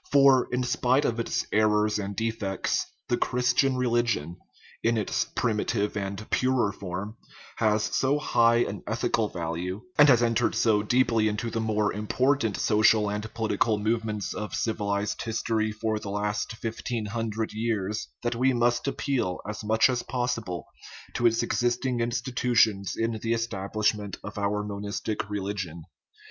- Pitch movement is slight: Yes, narrow, 2.3 semitones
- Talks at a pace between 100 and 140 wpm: No, average, 155 wpm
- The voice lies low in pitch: Yes, low, 110 Hz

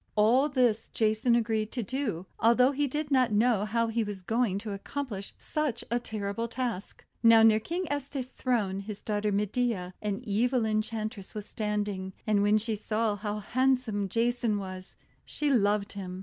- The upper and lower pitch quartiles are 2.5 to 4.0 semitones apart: Yes, average, 3.1 semitones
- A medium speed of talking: Yes, average, 165 wpm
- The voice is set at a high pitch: Yes, high, 220 Hz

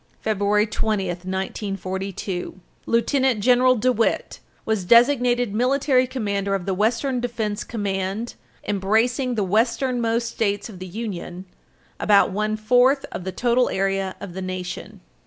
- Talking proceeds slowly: Yes, slow, 125 wpm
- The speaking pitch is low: No, high, 215 Hz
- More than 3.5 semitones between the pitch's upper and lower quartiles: Yes, average, 3.9 semitones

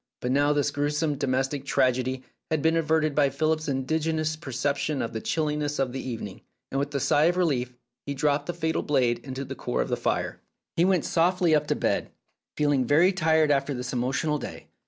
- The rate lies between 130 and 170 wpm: No, average, 200 wpm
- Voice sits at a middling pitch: Yes, medium, 145 Hz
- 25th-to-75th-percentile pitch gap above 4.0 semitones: No, average, 3.0 semitones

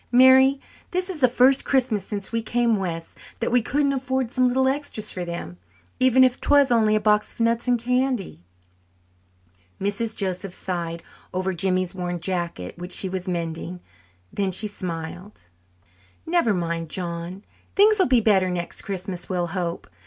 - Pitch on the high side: Yes, high, 205 Hz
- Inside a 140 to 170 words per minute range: Yes, average, 160 wpm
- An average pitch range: No, wide, 5.9 semitones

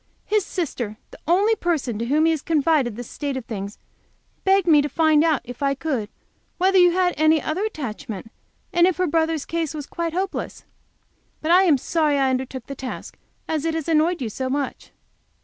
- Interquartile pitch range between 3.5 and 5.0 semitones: Yes, average, 4.5 semitones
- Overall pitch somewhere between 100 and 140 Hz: No, very high, 310 Hz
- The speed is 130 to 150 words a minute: No, average, 195 wpm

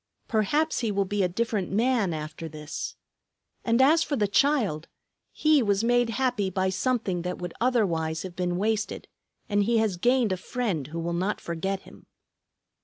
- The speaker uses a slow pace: No, average, 175 wpm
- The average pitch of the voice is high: Yes, high, 205 Hz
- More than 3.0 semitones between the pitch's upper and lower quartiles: Yes, average, 5.2 semitones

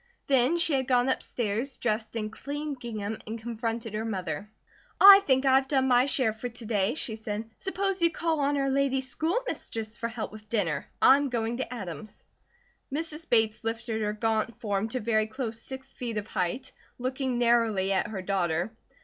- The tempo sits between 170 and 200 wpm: Yes, average, 185 wpm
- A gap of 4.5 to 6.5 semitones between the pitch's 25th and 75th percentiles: No, average, 3.6 semitones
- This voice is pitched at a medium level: No, high, 235 Hz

